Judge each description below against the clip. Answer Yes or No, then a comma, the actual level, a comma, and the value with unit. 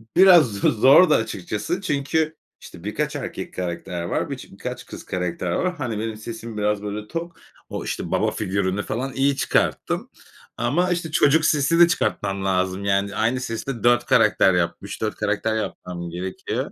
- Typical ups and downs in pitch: No, wide, 7.1 semitones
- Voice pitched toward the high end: No, low, 110 Hz